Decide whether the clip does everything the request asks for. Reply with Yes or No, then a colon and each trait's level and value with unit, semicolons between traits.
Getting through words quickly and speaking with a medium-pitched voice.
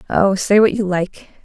No: fast, 210 wpm; high, 195 Hz